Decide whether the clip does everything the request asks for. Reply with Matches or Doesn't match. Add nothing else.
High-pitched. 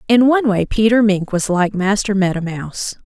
Matches